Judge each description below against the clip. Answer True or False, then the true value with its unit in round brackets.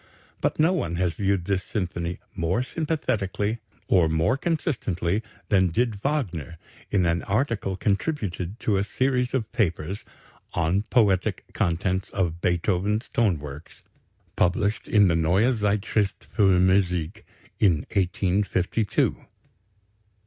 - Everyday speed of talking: False (120 wpm)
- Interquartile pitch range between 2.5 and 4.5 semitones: True (3.8 semitones)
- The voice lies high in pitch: False (95 Hz)